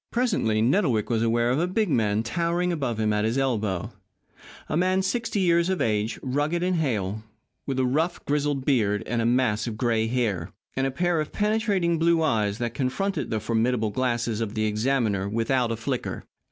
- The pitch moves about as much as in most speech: No, wide, 7.2 semitones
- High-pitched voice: No, low, 125 Hz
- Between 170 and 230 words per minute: Yes, average, 185 wpm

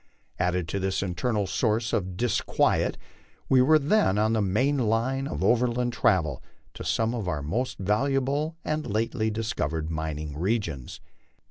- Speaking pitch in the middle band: No, low, 110 Hz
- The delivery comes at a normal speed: Yes, average, 145 wpm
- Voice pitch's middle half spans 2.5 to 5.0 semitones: No, wide, 5.6 semitones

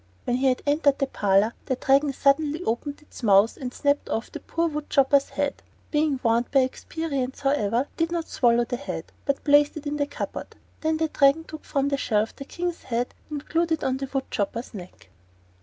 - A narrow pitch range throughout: No, average, 3.3 semitones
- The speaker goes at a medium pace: No, fast, 210 wpm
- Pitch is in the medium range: No, very high, 275 Hz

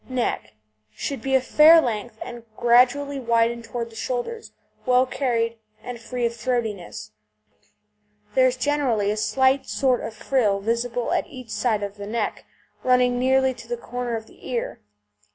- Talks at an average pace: Yes, average, 165 wpm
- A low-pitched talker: No, high, 245 Hz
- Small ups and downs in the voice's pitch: Yes, narrow, 2.1 semitones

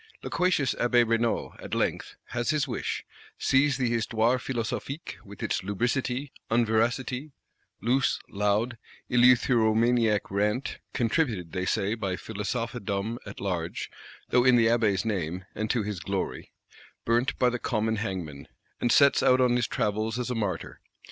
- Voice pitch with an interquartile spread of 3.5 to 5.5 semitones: No, average, 3.1 semitones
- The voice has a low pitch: Yes, low, 115 Hz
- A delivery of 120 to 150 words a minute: Yes, average, 140 wpm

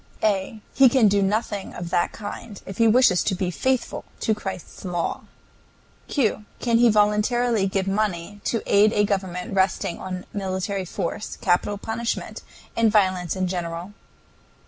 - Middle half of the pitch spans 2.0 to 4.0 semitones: Yes, average, 2.7 semitones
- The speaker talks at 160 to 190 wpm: No, average, 150 wpm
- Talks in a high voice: Yes, high, 200 Hz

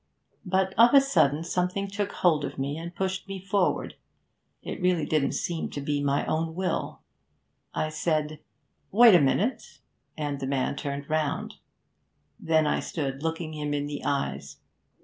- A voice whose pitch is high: No, medium, 155 Hz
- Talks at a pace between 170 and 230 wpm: No, average, 160 wpm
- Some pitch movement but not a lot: Yes, average, 4.2 semitones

